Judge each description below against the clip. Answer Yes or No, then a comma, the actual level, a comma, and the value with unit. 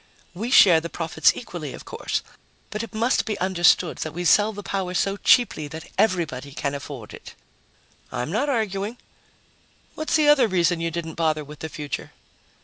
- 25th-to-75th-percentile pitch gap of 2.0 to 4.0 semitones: No, average, 5.3 semitones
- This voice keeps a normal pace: Yes, average, 175 wpm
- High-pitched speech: No, medium, 175 Hz